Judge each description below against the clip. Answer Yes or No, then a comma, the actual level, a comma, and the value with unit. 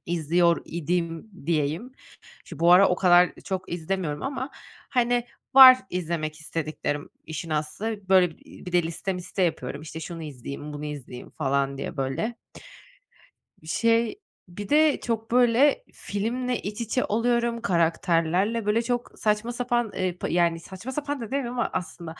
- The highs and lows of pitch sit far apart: Yes, wide, 6.2 semitones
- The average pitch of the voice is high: No, medium, 180 Hz